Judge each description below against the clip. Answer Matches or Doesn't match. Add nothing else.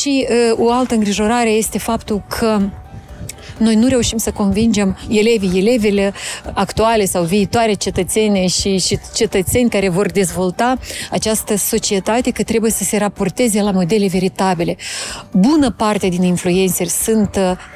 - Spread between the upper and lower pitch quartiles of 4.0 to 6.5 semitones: Doesn't match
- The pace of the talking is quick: Doesn't match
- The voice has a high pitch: Matches